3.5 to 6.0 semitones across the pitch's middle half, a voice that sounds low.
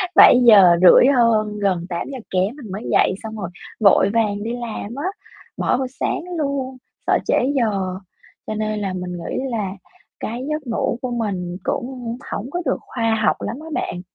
No: average, 4.2 semitones; high, 220 Hz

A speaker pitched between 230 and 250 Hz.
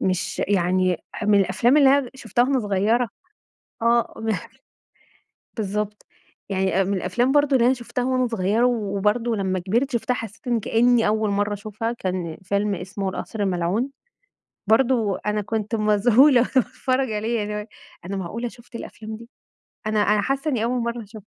No: high, 220 Hz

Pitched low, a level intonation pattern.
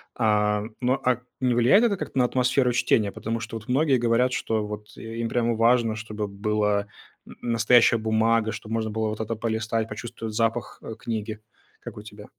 Yes: low, 115 Hz; narrow, 1.9 semitones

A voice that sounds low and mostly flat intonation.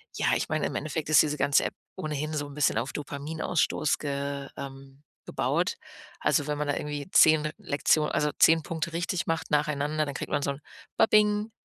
No: medium, 150 Hz; narrow, 1.9 semitones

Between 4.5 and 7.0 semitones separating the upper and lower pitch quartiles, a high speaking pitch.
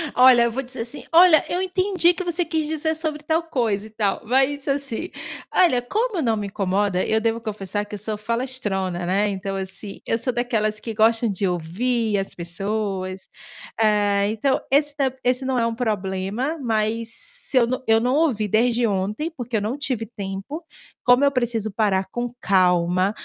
Yes: average, 4.9 semitones; high, 230 Hz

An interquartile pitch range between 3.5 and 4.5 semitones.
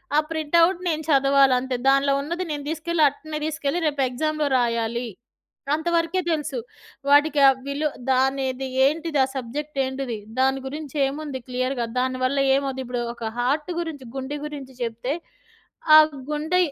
No: average, 2.9 semitones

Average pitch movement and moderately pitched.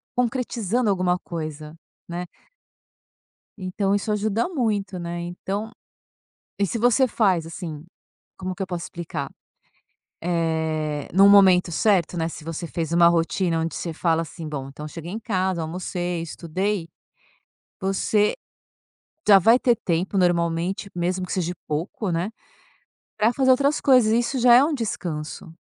Yes: average, 4.1 semitones; medium, 180 Hz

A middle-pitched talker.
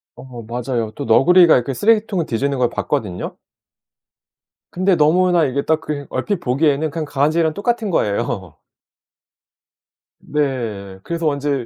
Yes: medium, 145 Hz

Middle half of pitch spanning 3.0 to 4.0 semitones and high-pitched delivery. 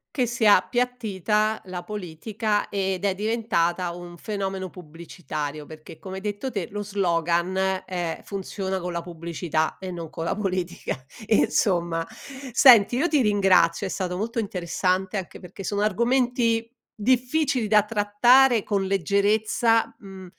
Yes: average, 3.7 semitones; high, 195 Hz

